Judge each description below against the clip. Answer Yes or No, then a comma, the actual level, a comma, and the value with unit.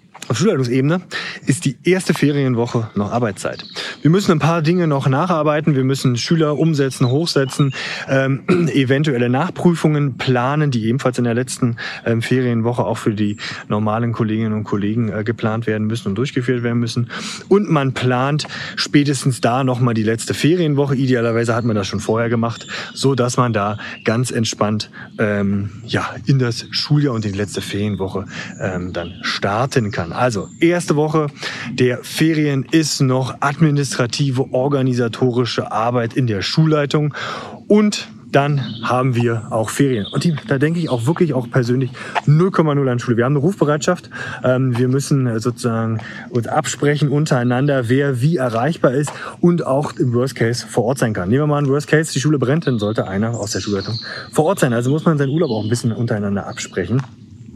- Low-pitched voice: Yes, low, 130 Hz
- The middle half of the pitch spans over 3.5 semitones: Yes, average, 4.1 semitones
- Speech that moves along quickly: No, average, 170 wpm